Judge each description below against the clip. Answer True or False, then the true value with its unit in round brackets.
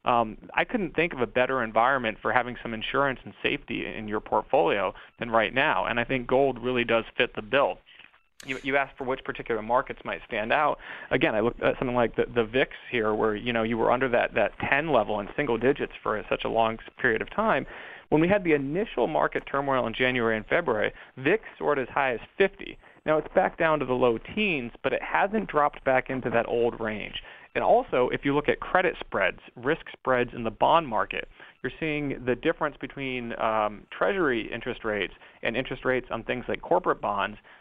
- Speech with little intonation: False (4.0 semitones)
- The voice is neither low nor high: False (130 Hz)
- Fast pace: True (215 wpm)